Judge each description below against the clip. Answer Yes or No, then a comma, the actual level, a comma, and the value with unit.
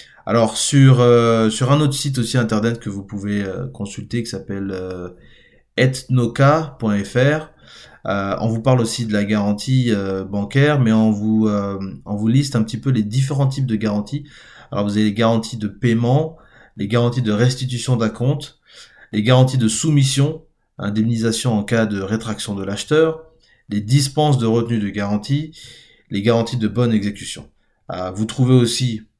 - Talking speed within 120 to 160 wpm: No, average, 170 wpm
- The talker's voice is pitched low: Yes, low, 115 Hz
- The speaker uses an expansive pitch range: No, average, 3.8 semitones